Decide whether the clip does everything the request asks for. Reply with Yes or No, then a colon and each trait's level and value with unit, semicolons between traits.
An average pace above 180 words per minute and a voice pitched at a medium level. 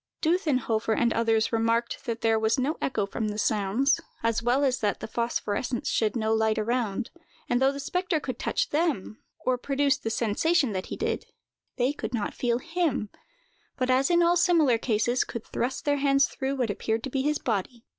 No: average, 195 wpm; high, 245 Hz